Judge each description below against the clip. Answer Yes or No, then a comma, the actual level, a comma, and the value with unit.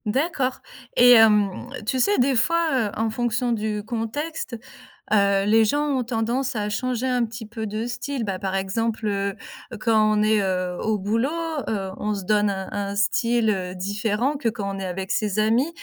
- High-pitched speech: Yes, high, 220 Hz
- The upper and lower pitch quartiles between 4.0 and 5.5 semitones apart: No, average, 3.2 semitones